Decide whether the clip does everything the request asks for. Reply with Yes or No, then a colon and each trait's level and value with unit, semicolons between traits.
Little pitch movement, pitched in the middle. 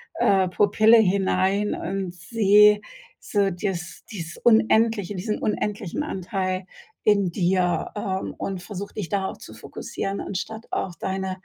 No: narrow, 2.1 semitones; high, 195 Hz